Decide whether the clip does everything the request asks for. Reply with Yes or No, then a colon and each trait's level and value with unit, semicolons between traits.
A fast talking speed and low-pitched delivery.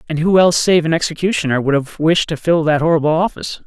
No: fast, 230 wpm; medium, 160 Hz